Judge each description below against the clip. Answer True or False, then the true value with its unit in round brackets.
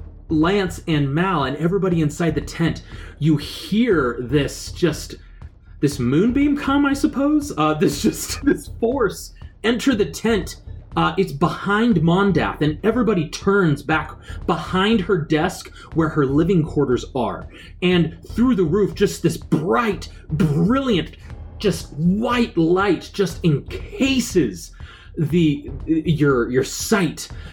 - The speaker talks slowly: True (125 wpm)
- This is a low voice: False (170 Hz)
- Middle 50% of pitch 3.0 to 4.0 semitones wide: False (4.8 semitones)